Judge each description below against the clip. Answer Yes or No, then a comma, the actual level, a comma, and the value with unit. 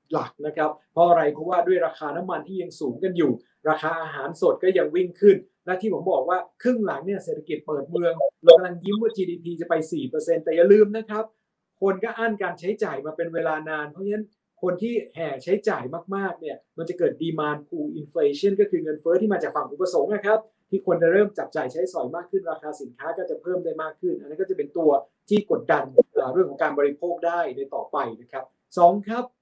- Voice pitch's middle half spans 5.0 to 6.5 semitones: No, average, 4.5 semitones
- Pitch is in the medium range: Yes, medium, 180 Hz